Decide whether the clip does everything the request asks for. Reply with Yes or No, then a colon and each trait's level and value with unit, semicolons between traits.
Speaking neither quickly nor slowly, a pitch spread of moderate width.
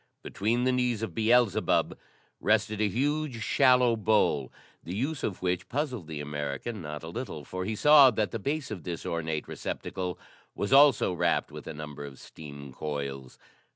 No: average, 170 wpm; wide, 8.1 semitones